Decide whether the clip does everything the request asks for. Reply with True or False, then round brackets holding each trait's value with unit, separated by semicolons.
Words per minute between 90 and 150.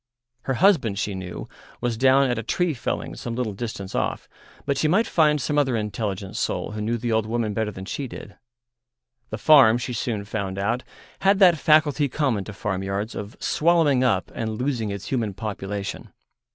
False (185 wpm)